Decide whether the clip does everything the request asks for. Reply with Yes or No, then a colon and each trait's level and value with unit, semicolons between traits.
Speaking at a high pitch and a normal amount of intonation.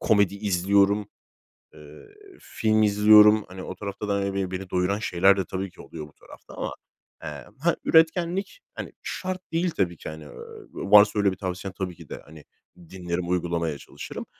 No: low, 100 Hz; average, 3.0 semitones